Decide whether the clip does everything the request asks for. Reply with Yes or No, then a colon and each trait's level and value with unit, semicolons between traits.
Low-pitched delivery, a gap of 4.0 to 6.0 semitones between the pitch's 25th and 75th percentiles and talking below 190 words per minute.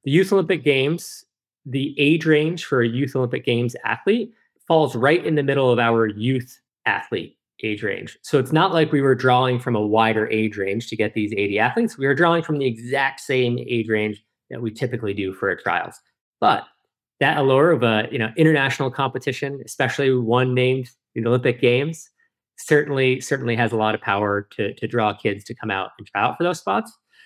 No: low, 130 Hz; average, 4.4 semitones; fast, 205 wpm